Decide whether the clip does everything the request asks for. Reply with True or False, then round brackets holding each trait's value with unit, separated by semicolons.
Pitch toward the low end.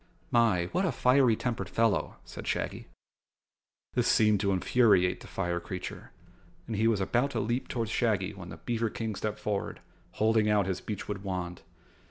True (105 Hz)